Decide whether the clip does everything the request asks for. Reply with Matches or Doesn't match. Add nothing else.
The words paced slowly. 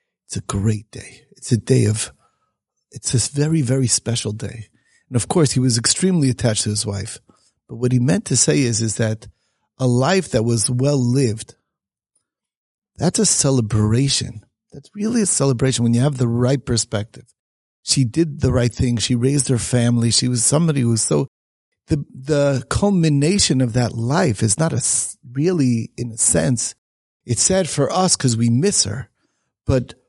Doesn't match